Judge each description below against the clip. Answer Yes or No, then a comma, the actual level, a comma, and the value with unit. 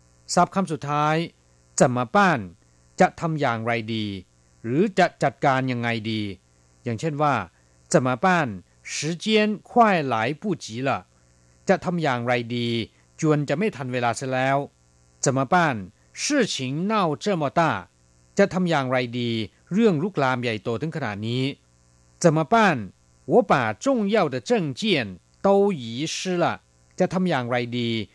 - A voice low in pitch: Yes, low, 130 Hz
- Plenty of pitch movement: Yes, wide, 8.5 semitones